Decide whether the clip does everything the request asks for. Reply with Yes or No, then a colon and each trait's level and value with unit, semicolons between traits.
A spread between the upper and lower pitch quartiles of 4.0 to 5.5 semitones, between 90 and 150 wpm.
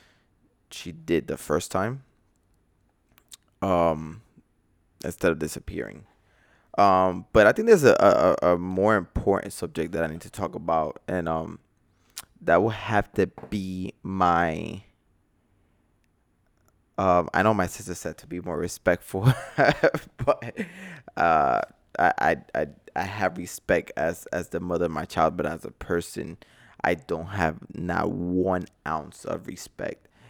No: average, 2.9 semitones; average, 140 wpm